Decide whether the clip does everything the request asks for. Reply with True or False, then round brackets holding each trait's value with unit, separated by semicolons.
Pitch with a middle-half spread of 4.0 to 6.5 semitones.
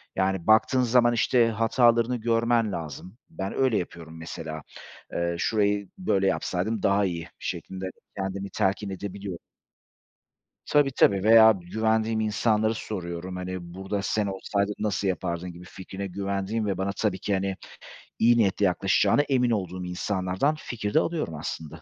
False (3.3 semitones)